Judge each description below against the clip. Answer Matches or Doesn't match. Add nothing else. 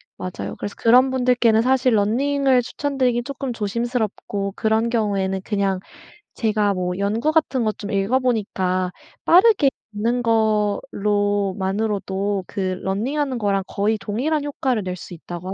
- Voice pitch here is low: Doesn't match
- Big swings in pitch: Doesn't match